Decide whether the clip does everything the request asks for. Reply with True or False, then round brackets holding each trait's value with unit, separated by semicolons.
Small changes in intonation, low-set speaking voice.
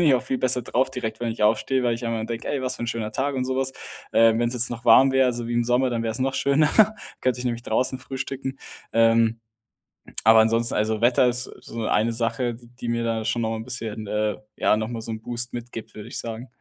True (2.1 semitones; 120 Hz)